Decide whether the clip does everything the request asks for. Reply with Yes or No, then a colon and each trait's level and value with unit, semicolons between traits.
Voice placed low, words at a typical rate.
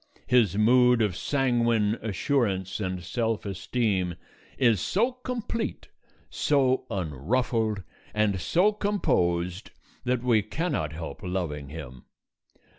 No: low, 110 Hz; slow, 105 wpm